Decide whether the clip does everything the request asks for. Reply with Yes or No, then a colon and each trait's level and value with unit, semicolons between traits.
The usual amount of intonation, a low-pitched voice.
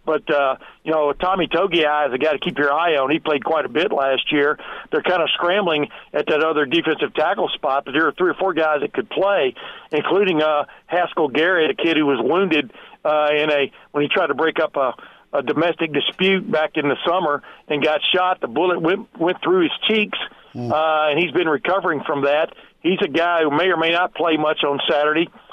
No: average, 3.6 semitones; medium, 155 Hz